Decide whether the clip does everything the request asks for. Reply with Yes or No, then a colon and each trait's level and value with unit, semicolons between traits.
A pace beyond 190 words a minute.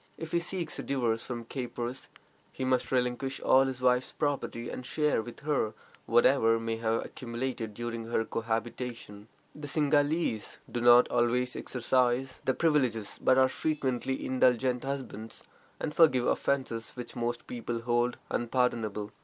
No: average, 145 wpm